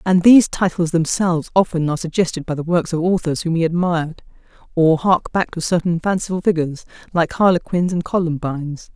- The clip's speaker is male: No, female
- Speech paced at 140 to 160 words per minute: No, average, 175 wpm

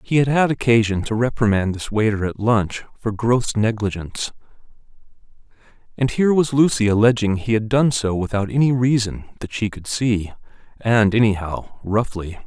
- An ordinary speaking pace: Yes, average, 155 wpm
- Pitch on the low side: Yes, low, 110 Hz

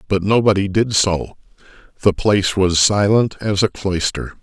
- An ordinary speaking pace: Yes, average, 150 wpm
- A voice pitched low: Yes, low, 100 Hz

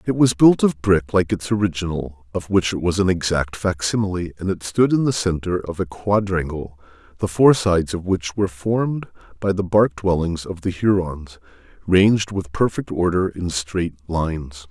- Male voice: Yes, male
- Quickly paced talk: No, average, 185 wpm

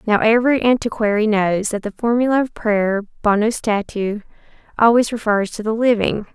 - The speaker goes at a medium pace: Yes, average, 150 wpm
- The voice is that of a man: No, female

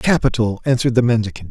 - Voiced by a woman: No, male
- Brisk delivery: No, average, 160 wpm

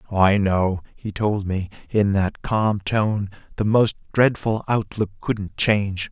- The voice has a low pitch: Yes, low, 100 Hz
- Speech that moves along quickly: No, average, 145 wpm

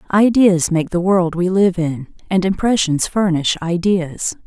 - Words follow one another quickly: No, average, 150 wpm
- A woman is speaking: Yes, female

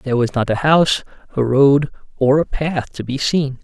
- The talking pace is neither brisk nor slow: No, fast, 215 wpm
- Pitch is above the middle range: No, medium, 140 Hz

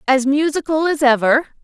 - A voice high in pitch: Yes, very high, 280 Hz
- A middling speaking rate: Yes, average, 145 wpm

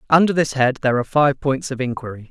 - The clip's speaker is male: Yes, male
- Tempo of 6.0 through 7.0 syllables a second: Yes, 6.8 syllables/s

